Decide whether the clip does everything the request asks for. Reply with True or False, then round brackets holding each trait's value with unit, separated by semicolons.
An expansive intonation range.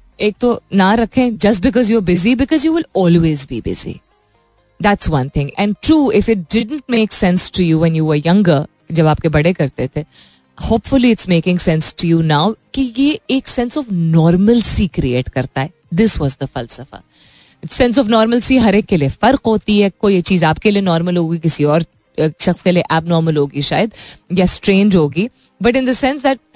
True (6.5 semitones)